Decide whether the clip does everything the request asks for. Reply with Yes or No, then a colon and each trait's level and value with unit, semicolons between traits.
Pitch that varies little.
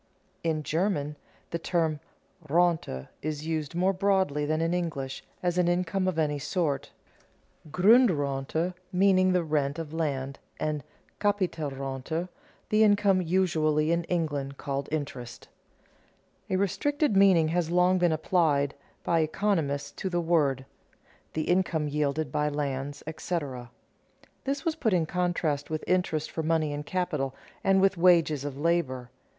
No: average, 3.7 semitones